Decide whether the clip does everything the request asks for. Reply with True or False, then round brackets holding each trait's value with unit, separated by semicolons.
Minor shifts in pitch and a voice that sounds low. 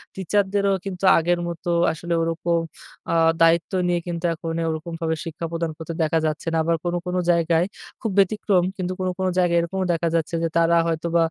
False (1.7 semitones; 170 Hz)